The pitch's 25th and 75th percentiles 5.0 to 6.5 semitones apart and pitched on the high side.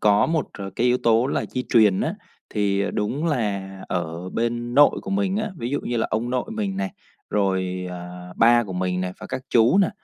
No: average, 5.3 semitones; low, 115 Hz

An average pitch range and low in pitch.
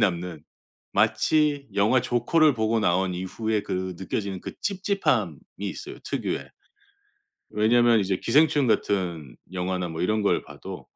Yes: average, 4.9 semitones; low, 105 Hz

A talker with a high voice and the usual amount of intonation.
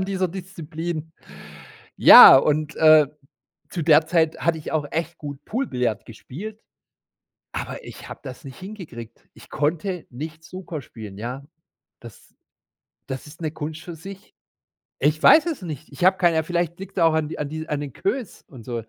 No: medium, 160 Hz; average, 3.4 semitones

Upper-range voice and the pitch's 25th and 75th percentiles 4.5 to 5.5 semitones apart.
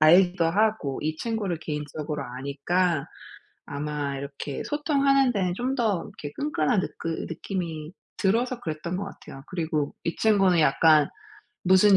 No: medium, 170 Hz; average, 5.2 semitones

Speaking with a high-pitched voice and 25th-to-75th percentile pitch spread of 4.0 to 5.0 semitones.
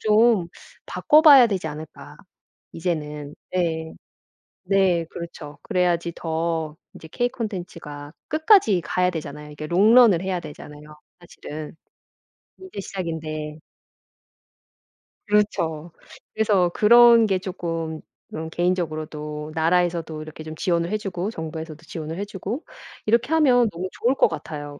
No: medium, 170 Hz; average, 4.6 semitones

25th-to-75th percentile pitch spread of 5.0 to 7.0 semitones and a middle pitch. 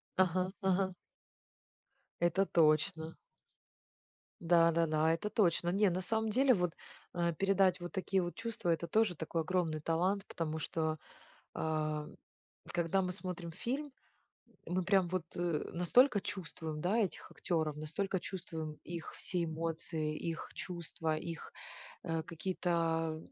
No: average, 2.7 semitones; medium, 175 Hz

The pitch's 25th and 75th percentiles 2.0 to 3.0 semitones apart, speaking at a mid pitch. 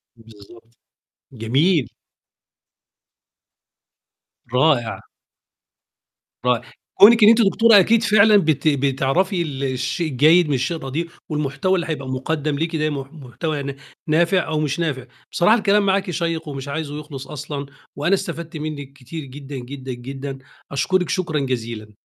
No: average, 4.2 semitones; medium, 150 Hz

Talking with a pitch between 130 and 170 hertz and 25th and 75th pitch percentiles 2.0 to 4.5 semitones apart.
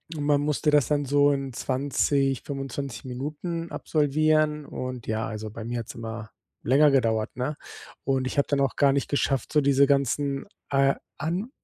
Yes: medium, 140 Hz; narrow, 2.4 semitones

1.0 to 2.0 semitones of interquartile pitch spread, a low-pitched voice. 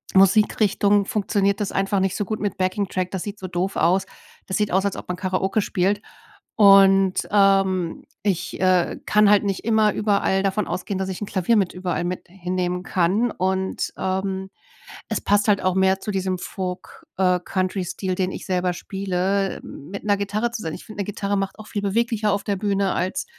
No: narrow, 1.6 semitones; high, 195 Hz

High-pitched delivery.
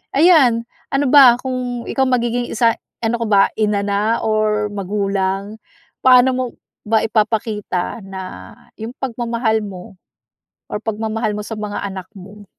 Yes: high, 220 Hz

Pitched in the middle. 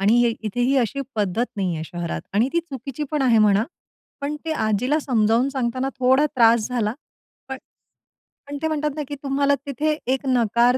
No: very high, 250 Hz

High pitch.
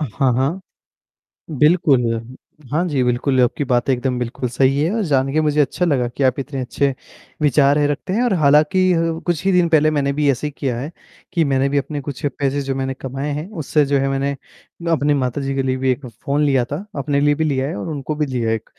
No: medium, 140 Hz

